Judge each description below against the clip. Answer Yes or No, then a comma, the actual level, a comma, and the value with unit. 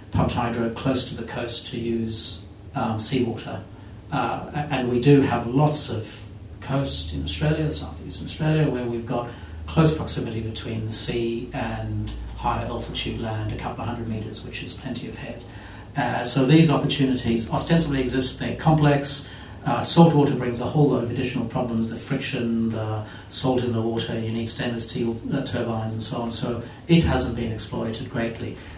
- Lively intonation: No, average, 2.9 semitones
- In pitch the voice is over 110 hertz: Yes, low, 120 Hz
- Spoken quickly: No, average, 180 wpm